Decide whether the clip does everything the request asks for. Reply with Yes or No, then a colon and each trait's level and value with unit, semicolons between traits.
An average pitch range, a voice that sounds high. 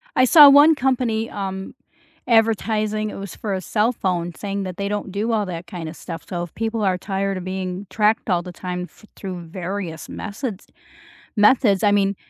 Yes: average, 3.1 semitones; high, 200 Hz